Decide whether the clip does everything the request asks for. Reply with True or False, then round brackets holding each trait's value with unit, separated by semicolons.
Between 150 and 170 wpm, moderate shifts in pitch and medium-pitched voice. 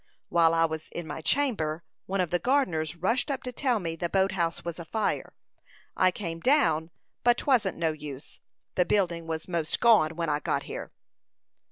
False (185 wpm; 4.6 semitones; 170 Hz)